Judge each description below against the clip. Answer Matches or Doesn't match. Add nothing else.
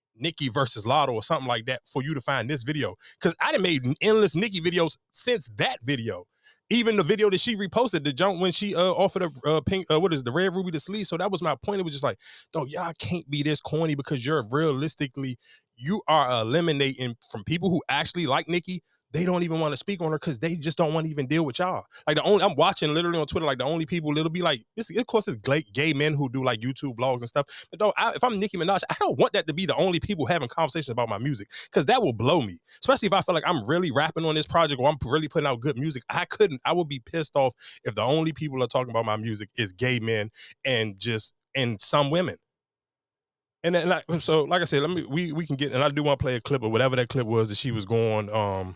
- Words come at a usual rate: Doesn't match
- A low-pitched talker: Doesn't match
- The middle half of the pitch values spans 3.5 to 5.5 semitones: Matches